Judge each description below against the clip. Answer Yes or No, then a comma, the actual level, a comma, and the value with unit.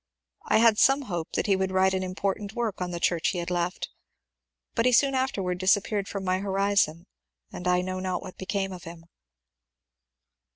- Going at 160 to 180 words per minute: No, average, 190 wpm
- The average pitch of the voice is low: No, high, 190 Hz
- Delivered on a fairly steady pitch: Yes, narrow, 2.1 semitones